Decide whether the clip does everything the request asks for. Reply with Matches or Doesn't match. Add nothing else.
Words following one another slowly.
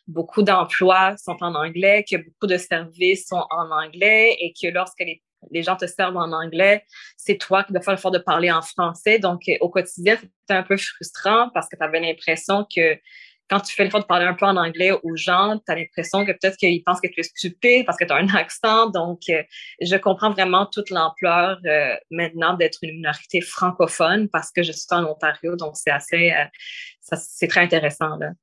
Doesn't match